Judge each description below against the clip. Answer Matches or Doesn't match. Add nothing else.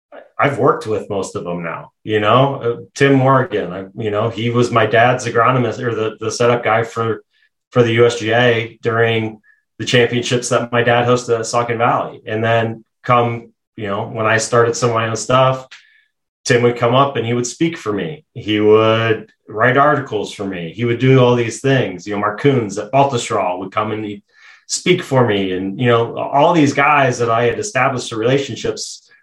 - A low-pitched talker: Matches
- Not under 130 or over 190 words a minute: Doesn't match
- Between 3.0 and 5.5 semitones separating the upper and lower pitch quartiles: Doesn't match